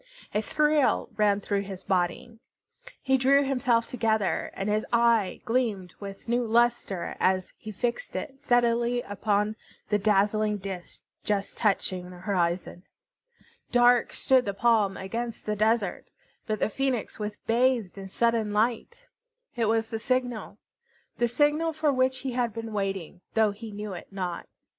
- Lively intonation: No, average, 3.3 semitones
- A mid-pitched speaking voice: No, high, 220 Hz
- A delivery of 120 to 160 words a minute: Yes, average, 150 wpm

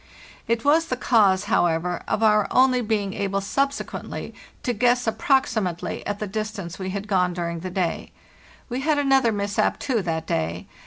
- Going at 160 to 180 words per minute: Yes, average, 165 wpm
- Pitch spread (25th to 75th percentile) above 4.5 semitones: Yes, average, 5.0 semitones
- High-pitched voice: Yes, high, 210 Hz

